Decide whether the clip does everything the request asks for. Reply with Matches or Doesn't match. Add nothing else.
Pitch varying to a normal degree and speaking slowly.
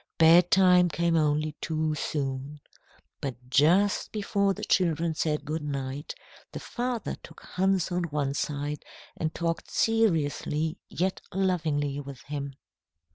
Matches